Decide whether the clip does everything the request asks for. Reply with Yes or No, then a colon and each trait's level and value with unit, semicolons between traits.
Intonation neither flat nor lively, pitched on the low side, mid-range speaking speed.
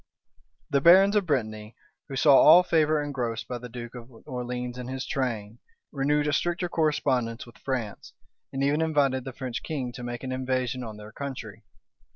Yes: average, 3.4 semitones; low, 130 Hz; average, 180 wpm